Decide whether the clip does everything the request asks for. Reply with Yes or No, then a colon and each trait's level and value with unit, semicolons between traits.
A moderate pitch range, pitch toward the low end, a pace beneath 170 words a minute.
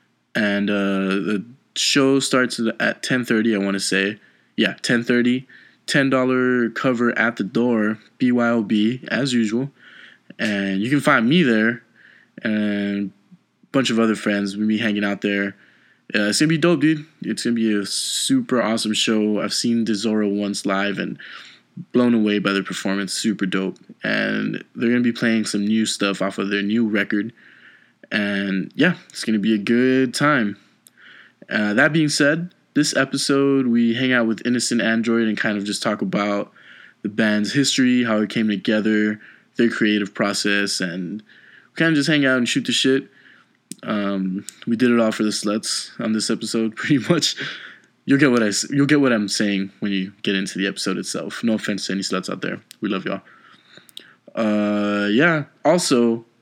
No: average, 3.2 semitones; low, 110 Hz; average, 180 wpm